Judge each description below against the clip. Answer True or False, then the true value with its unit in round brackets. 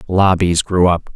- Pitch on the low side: True (90 Hz)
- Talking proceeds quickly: False (155 wpm)